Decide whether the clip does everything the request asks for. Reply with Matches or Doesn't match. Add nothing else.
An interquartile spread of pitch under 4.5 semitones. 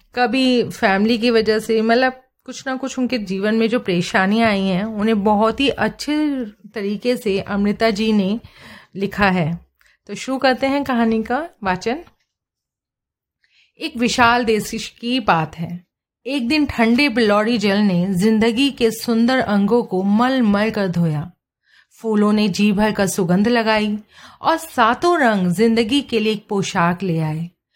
Matches